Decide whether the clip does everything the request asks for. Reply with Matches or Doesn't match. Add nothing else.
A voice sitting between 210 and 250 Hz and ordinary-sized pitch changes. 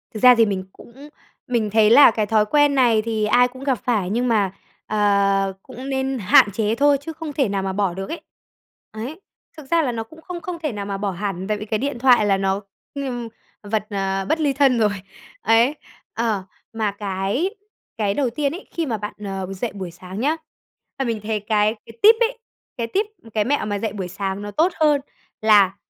Matches